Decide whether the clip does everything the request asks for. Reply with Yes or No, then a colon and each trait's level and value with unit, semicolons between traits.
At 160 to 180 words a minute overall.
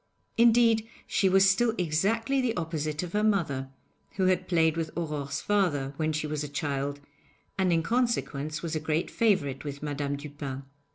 Yes: average, 170 wpm